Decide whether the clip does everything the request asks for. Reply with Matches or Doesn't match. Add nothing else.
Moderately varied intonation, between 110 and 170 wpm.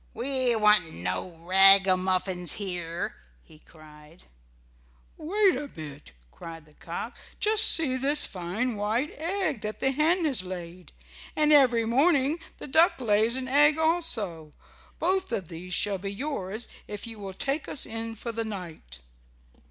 Doesn't match